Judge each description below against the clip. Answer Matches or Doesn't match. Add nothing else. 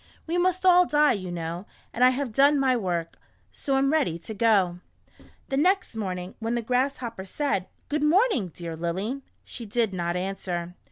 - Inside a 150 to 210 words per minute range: Matches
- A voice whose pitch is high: Matches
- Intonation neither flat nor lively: Doesn't match